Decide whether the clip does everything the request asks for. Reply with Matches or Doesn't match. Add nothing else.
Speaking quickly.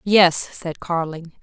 Doesn't match